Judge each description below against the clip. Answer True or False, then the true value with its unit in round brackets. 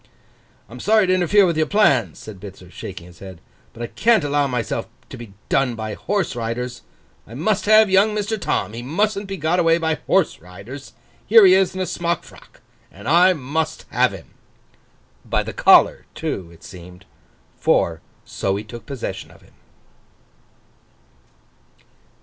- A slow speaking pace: False (165 wpm)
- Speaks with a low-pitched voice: False (145 Hz)